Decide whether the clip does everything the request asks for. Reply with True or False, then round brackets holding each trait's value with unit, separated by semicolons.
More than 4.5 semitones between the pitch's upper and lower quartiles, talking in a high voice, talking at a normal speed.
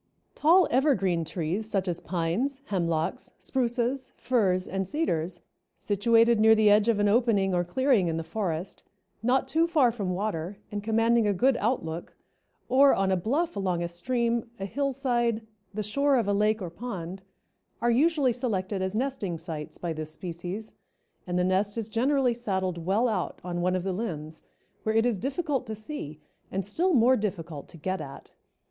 True (5.3 semitones; 210 Hz; 175 wpm)